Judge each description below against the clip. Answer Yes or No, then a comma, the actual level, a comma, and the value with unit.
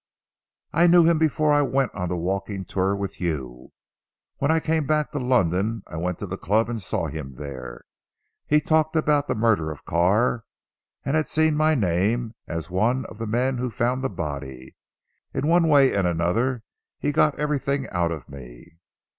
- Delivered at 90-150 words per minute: No, average, 185 wpm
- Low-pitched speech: Yes, low, 115 Hz